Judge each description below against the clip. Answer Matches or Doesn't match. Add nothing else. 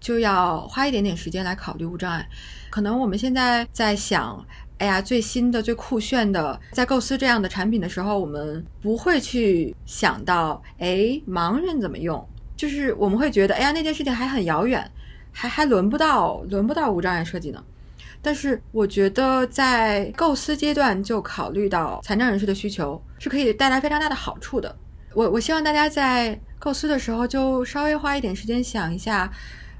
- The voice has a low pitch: Doesn't match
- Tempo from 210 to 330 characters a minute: Matches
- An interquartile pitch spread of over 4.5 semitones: Matches